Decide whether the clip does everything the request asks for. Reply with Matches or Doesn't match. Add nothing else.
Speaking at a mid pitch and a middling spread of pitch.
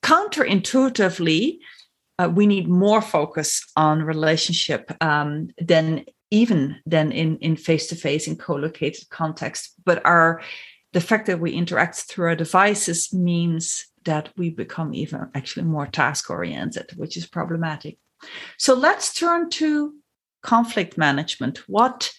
Matches